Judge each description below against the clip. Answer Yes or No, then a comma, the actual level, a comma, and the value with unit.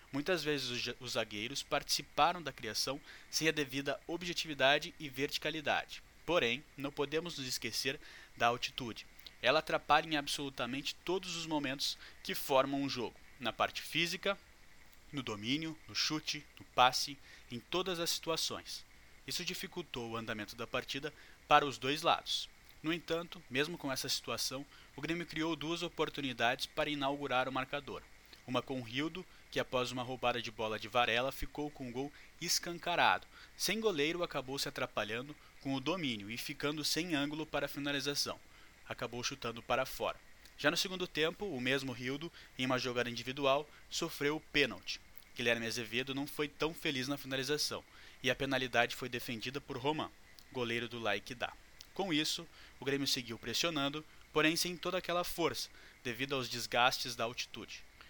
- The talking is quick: No, average, 155 wpm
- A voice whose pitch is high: No, medium, 140 Hz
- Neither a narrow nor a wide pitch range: Yes, average, 3.7 semitones